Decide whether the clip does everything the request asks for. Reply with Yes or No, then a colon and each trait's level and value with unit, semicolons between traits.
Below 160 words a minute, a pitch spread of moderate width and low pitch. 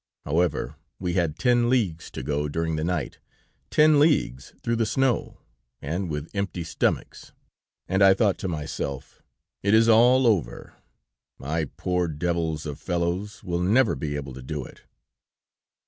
No: average, 150 wpm; wide, 5.9 semitones; very low, 85 Hz